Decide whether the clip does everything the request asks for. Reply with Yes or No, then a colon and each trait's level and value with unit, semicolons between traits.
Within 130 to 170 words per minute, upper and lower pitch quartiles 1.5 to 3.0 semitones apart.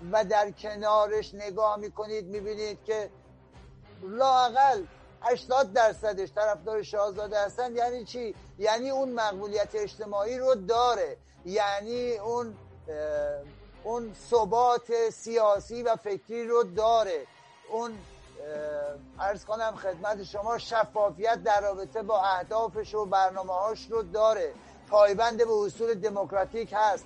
No: average, 110 wpm; narrow, 2.5 semitones